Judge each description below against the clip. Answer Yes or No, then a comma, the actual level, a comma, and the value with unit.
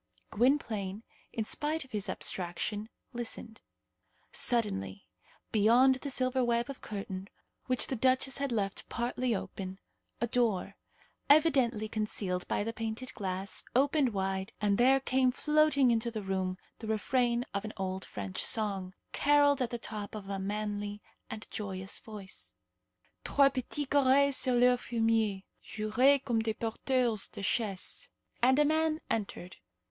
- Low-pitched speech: No, high, 225 Hz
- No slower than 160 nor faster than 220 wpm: No, average, 140 wpm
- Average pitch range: Yes, average, 4.3 semitones